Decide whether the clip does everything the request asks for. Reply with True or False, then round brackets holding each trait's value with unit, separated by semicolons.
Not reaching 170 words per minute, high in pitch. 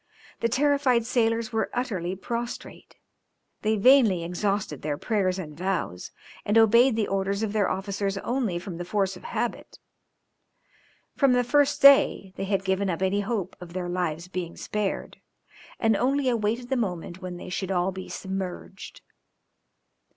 True (155 wpm; 200 Hz)